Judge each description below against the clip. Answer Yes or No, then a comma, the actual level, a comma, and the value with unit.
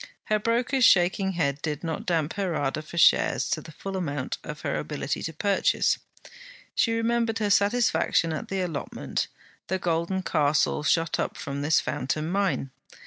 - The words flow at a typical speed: Yes, average, 165 wpm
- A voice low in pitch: No, medium, 175 Hz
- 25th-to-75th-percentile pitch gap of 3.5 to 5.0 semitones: Yes, average, 4.7 semitones